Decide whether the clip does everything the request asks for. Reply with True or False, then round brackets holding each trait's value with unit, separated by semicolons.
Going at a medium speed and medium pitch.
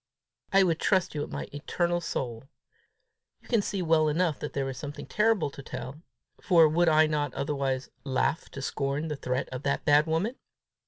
True (180 wpm; 150 Hz)